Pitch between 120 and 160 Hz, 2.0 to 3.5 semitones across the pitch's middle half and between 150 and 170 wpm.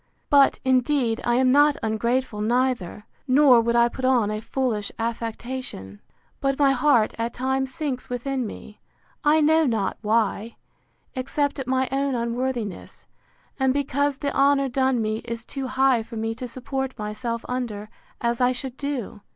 No: very high, 255 Hz; average, 2.7 semitones; average, 160 wpm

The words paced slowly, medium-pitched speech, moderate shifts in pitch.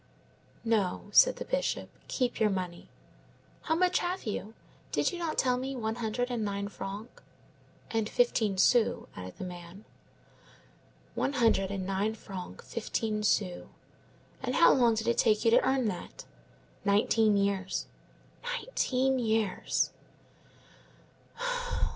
No: slow, 130 wpm; high, 220 Hz; average, 3.8 semitones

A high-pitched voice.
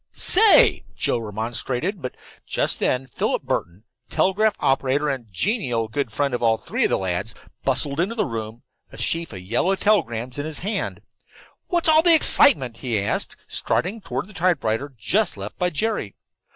No: low, 135 Hz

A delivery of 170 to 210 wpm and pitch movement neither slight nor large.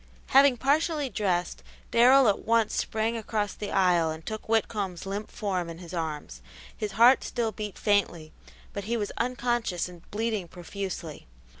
No: average, 155 wpm; average, 4.4 semitones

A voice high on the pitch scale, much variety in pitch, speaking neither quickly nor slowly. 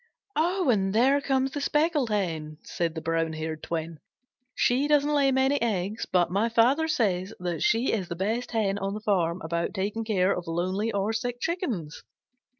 Yes: high, 210 Hz; wide, 6.8 semitones; average, 175 wpm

